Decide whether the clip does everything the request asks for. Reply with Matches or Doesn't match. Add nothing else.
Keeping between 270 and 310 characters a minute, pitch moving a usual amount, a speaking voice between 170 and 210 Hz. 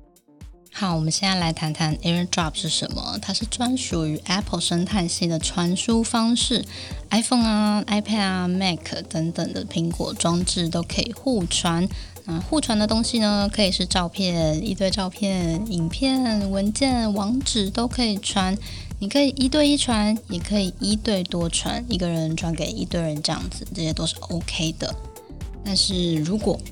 Matches